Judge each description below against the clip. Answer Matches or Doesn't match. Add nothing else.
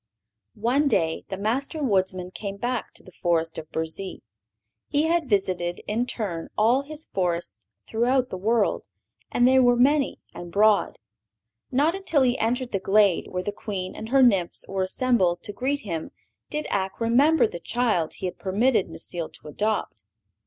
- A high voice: Matches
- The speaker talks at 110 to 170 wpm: Matches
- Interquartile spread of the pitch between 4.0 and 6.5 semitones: Matches